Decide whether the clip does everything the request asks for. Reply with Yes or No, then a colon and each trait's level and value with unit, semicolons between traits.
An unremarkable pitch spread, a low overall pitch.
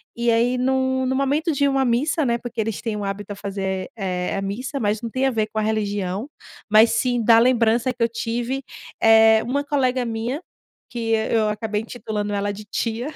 No: average, 3.2 semitones; high, 230 Hz